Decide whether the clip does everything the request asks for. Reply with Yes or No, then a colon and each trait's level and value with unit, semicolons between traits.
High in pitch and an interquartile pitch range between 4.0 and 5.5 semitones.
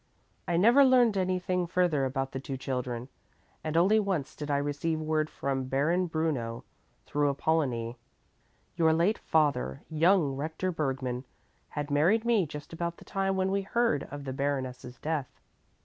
No: medium, 155 Hz; average, 5.1 semitones